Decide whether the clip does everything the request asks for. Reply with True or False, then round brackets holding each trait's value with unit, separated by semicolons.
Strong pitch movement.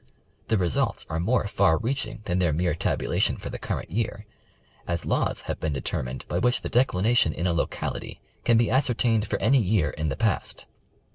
True (6.0 semitones)